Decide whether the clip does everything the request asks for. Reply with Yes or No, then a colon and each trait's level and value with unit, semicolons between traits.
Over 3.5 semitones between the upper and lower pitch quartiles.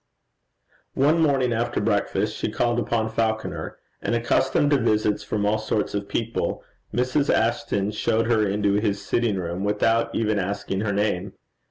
No: narrow, 2.4 semitones